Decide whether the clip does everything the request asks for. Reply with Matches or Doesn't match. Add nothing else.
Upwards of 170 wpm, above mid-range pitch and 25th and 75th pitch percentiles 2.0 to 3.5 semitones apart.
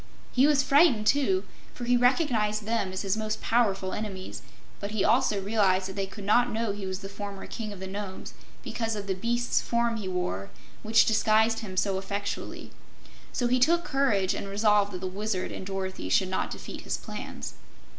Matches